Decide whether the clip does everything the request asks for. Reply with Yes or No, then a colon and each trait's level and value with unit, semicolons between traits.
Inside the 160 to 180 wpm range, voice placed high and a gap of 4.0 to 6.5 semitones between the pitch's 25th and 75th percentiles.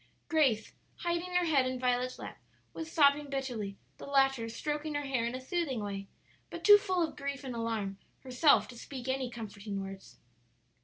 Yes: average, 175 wpm; very high, 260 Hz; average, 4.4 semitones